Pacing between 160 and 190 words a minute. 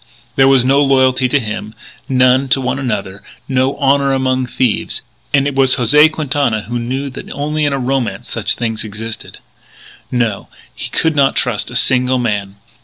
Yes: average, 175 wpm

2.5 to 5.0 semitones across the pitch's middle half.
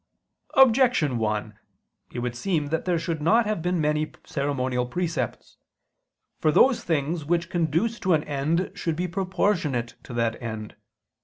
No: wide, 5.6 semitones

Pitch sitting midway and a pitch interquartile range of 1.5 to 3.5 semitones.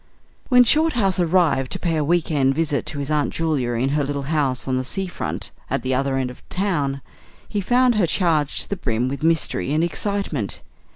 No: medium, 155 Hz; average, 5.1 semitones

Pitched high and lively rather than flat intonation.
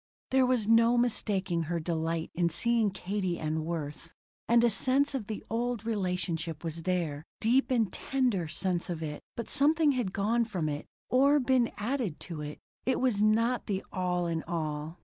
Yes: high, 195 Hz; wide, 6.2 semitones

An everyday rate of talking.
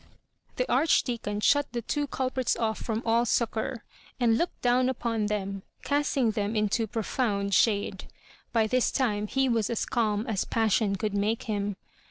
Yes: average, 165 wpm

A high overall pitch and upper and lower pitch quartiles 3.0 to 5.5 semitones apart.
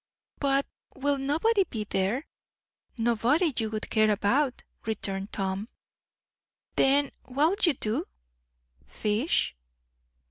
Yes: high, 245 Hz; average, 5.2 semitones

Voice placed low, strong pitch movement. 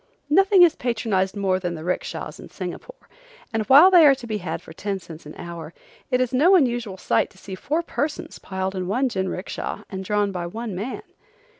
No: high, 210 Hz; wide, 6.1 semitones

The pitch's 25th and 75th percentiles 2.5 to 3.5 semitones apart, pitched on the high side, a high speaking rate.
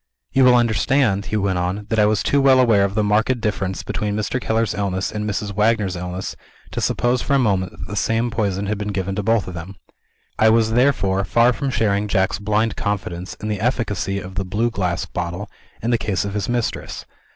No: average, 2.8 semitones; low, 105 Hz; fast, 220 wpm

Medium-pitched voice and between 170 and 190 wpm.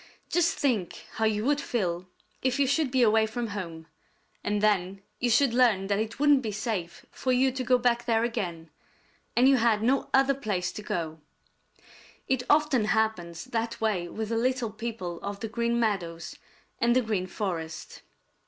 No: high, 225 Hz; average, 180 wpm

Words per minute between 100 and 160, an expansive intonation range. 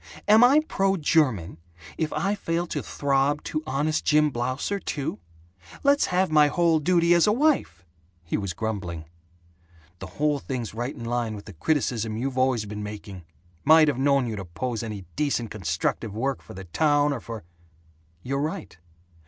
No: average, 170 wpm; wide, 6.7 semitones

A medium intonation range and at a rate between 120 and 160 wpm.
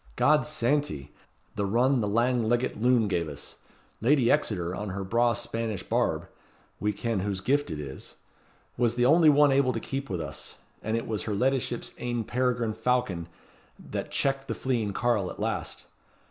No: average, 3.8 semitones; average, 175 wpm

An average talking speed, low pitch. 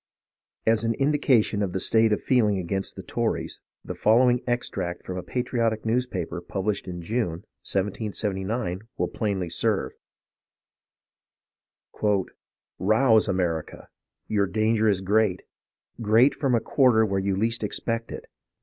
No: slow, 130 wpm; low, 110 Hz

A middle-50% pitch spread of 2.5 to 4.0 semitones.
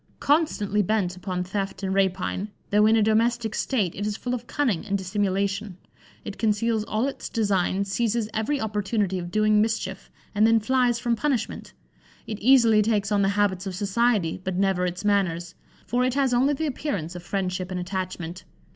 Yes: average, 3.2 semitones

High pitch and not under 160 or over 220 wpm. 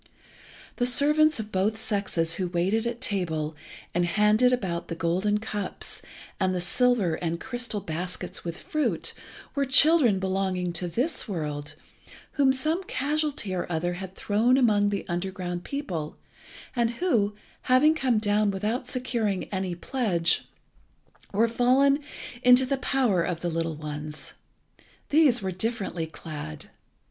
No: high, 205 Hz; slow, 135 wpm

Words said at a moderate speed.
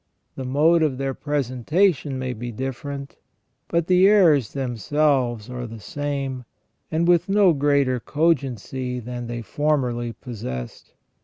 No: slow, 130 wpm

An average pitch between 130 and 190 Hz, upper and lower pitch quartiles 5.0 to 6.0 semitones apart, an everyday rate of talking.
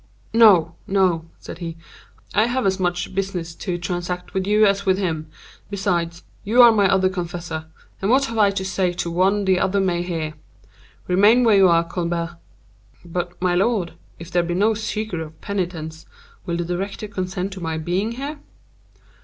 No: medium, 185 Hz; average, 2.7 semitones; average, 175 wpm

